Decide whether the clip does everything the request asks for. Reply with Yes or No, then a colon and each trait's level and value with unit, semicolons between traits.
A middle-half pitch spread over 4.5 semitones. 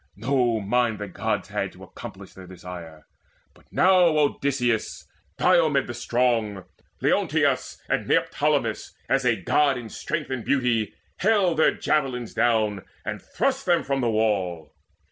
Yes: average, 5.1 semitones